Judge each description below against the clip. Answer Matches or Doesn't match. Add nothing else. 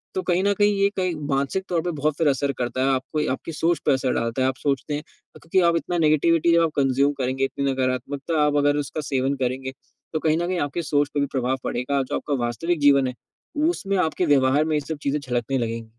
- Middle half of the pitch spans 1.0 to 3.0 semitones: Doesn't match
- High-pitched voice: Doesn't match